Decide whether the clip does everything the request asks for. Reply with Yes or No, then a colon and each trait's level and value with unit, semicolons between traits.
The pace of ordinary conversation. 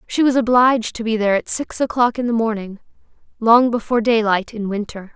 Yes: average, 185 wpm